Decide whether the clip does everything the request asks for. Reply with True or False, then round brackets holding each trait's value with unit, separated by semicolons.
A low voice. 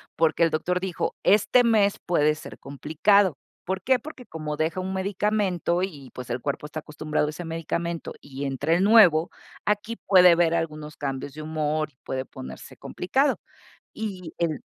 False (165 Hz)